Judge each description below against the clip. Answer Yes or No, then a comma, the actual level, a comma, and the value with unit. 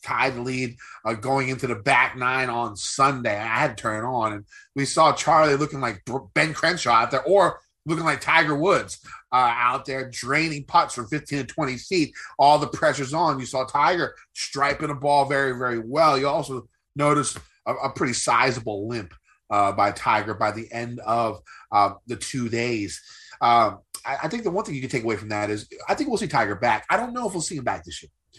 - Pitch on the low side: Yes, low, 130 Hz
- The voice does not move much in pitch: No, average, 4.1 semitones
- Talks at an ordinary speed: No, fast, 220 wpm